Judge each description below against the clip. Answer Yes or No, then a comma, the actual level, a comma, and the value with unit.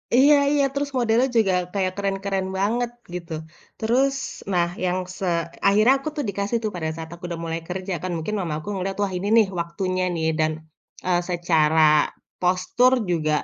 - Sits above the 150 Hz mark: Yes, high, 190 Hz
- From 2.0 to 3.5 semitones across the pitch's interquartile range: No, average, 4.2 semitones